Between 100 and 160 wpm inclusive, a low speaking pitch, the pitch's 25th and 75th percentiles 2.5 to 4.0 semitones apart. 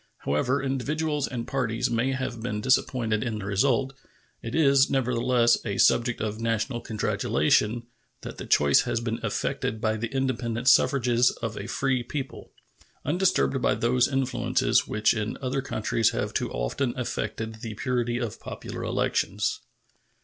Yes: average, 150 wpm; low, 120 Hz; average, 2.9 semitones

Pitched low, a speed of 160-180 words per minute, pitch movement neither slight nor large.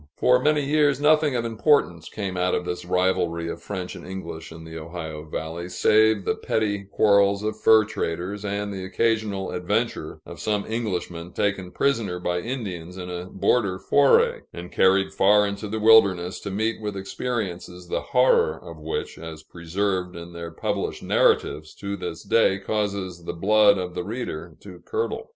Yes: very low, 95 Hz; average, 170 wpm; average, 3.6 semitones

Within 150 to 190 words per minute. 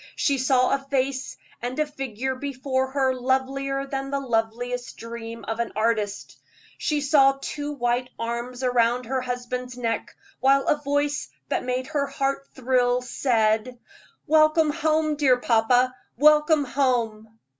No: average, 140 wpm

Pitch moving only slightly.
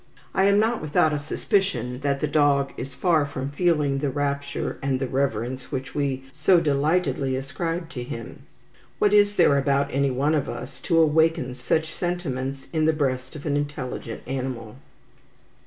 No: average, 3.2 semitones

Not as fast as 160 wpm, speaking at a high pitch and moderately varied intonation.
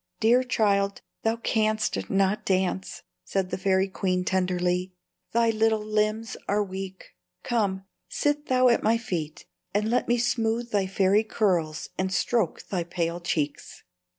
Yes: average, 145 wpm; high, 200 Hz; average, 3.3 semitones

